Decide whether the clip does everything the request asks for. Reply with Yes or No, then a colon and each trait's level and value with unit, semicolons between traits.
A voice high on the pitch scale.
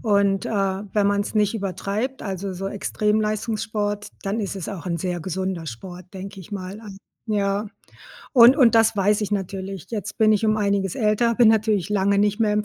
Yes: high, 205 Hz